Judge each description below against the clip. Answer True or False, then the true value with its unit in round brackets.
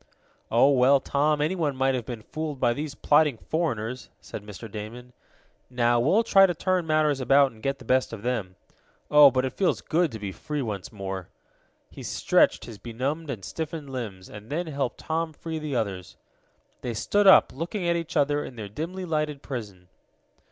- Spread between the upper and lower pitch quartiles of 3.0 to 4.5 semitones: False (5.2 semitones)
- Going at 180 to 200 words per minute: True (185 wpm)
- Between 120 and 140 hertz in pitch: True (135 Hz)